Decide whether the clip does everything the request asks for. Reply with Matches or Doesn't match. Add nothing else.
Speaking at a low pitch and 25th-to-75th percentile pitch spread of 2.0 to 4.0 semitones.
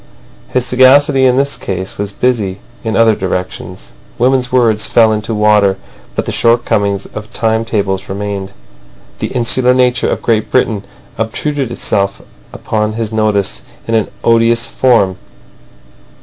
Matches